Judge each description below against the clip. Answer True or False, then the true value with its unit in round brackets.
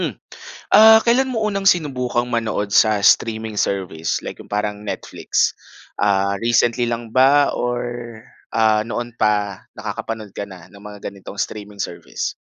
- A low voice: True (110 Hz)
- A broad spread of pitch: False (3.1 semitones)